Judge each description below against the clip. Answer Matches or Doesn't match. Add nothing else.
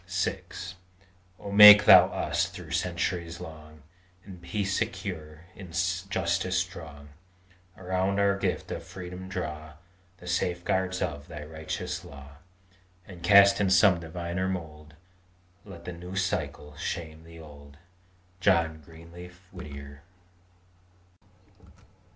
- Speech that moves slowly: Matches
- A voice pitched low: Matches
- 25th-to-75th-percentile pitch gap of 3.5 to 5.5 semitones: Doesn't match